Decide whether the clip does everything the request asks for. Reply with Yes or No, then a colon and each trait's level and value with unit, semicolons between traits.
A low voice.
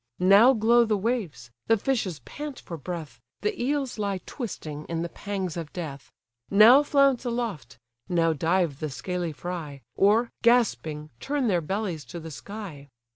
No: medium, 185 Hz